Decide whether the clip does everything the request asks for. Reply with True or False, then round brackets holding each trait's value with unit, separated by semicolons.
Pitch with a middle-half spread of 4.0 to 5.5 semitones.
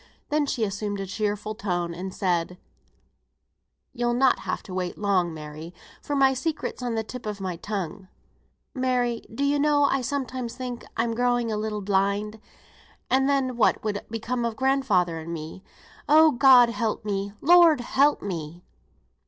True (5.1 semitones)